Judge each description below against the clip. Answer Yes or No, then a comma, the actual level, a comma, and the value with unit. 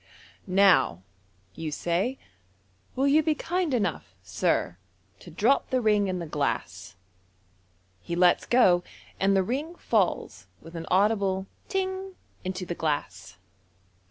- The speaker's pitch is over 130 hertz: Yes, high, 190 Hz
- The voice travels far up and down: Yes, wide, 7.5 semitones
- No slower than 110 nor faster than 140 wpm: Yes, slow, 135 wpm